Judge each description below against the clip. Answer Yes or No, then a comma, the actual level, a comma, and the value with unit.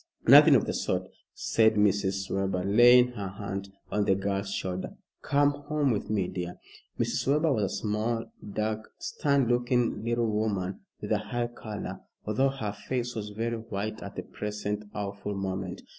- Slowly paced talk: No, average, 165 wpm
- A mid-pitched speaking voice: No, low, 105 Hz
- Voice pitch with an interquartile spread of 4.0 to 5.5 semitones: No, average, 3.2 semitones